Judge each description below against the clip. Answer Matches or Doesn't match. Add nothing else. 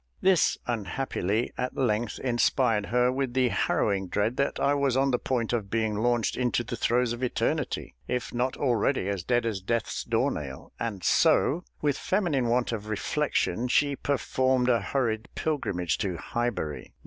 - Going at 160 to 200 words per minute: Matches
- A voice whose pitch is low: Matches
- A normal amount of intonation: Matches